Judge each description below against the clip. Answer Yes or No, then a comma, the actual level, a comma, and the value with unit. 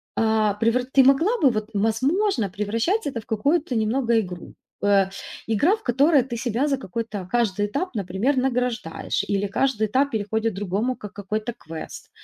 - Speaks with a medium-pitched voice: No, high, 225 Hz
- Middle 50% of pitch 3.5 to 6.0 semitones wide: Yes, average, 4.5 semitones